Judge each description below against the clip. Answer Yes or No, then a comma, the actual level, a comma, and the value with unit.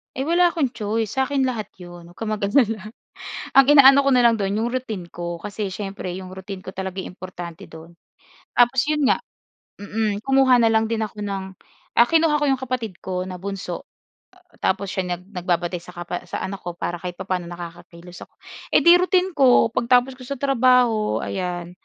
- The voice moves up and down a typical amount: No, wide, 5.9 semitones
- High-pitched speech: Yes, high, 210 Hz